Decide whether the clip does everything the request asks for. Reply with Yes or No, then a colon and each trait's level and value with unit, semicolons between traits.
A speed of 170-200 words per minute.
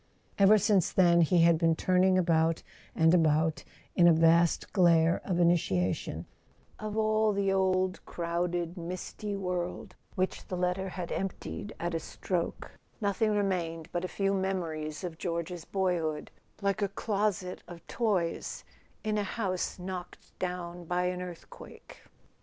No: average, 145 wpm